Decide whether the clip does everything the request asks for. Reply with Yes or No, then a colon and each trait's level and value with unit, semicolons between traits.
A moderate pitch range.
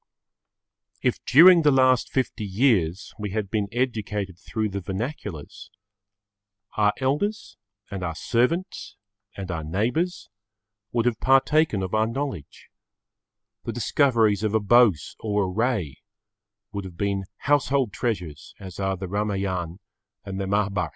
Yes: average, 4.8 semitones